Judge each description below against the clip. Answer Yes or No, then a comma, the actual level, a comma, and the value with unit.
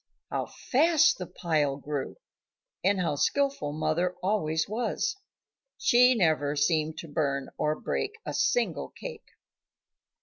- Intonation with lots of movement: Yes, wide, 8.5 semitones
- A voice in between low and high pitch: Yes, medium, 165 Hz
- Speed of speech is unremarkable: No, slow, 125 wpm